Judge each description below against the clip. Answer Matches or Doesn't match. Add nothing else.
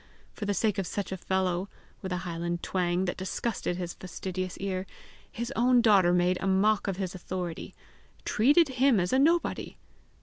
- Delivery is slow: Doesn't match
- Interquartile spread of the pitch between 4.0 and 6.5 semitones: Doesn't match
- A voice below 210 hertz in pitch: Matches